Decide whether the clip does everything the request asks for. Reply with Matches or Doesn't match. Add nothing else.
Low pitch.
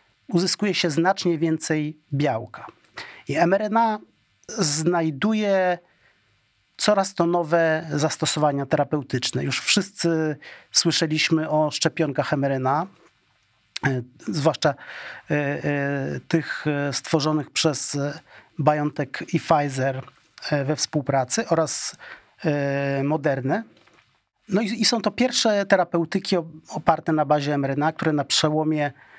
Doesn't match